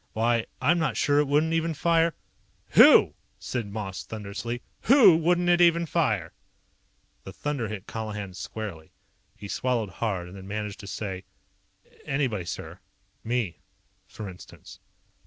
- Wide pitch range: Yes, wide, 7.8 semitones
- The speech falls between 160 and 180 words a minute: No, average, 140 wpm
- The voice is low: Yes, low, 115 Hz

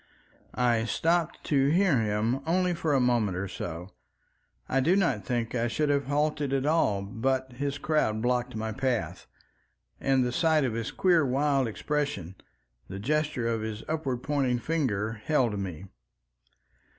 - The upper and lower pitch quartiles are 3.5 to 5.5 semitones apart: Yes, average, 4.9 semitones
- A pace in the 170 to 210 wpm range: No, average, 155 wpm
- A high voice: No, low, 130 Hz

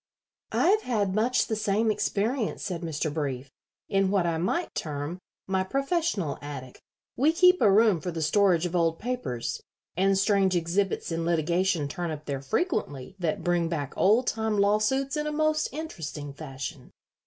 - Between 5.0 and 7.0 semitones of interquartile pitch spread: Yes, wide, 5.5 semitones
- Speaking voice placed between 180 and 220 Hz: Yes, high, 190 Hz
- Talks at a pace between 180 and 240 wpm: No, average, 165 wpm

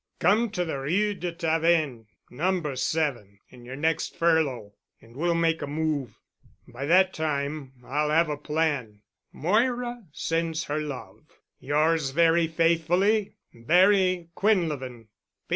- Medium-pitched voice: Yes, medium, 160 Hz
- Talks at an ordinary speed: No, slow, 125 wpm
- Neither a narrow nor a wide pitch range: Yes, average, 3.7 semitones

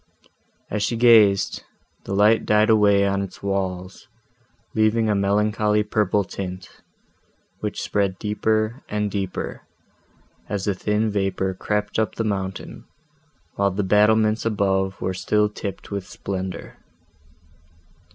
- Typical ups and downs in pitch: No, narrow, 1.6 semitones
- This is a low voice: Yes, low, 105 Hz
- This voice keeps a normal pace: No, slow, 120 wpm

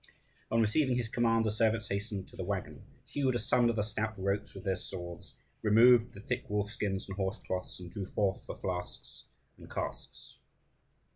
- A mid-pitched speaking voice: No, low, 105 Hz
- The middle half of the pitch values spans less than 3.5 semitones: Yes, average, 2.9 semitones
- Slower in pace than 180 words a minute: Yes, average, 170 wpm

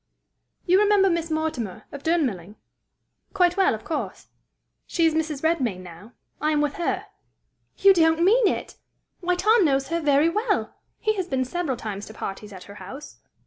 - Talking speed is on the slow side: No, average, 175 wpm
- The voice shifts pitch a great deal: Yes, wide, 6.6 semitones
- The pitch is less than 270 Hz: No, very high, 315 Hz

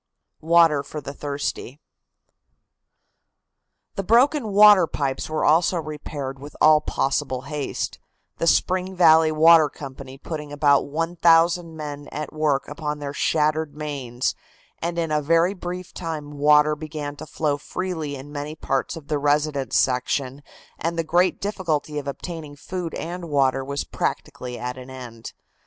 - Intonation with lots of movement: No, average, 2.7 semitones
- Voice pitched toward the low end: No, medium, 150 Hz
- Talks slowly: No, average, 145 wpm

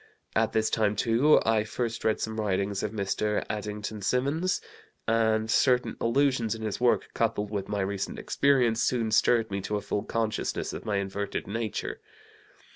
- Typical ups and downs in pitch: No, narrow, 2.0 semitones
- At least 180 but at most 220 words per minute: No, average, 165 wpm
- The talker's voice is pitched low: Yes, low, 110 Hz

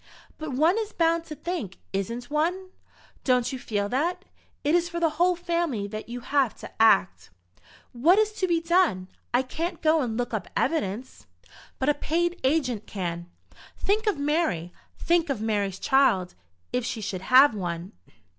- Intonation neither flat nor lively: No, wide, 7.6 semitones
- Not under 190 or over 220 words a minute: No, average, 170 wpm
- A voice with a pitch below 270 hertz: No, very high, 275 Hz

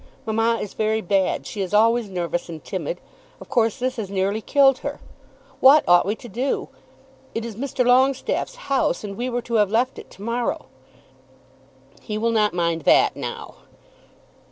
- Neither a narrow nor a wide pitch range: Yes, average, 3.8 semitones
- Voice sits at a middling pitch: No, high, 225 Hz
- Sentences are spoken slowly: No, average, 175 wpm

